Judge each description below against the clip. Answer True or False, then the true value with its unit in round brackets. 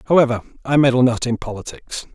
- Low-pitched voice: True (125 Hz)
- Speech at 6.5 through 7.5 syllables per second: True (6.6 syllables/s)